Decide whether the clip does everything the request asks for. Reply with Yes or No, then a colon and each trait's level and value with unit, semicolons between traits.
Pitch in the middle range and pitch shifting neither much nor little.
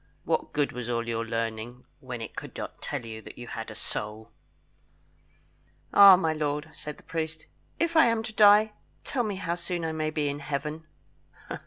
No: medium, 150 Hz; wide, 7.1 semitones